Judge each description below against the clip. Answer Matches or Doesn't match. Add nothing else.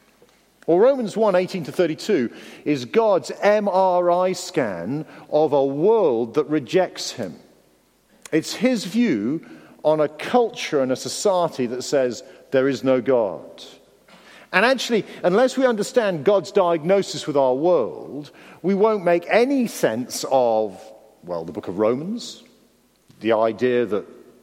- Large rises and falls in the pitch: Matches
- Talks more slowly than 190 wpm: Matches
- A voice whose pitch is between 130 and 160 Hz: Doesn't match